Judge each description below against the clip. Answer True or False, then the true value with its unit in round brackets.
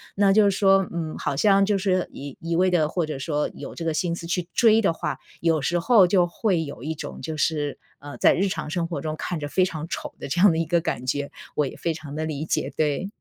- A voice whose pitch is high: False (165 Hz)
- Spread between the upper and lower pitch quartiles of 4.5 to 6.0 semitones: False (3.5 semitones)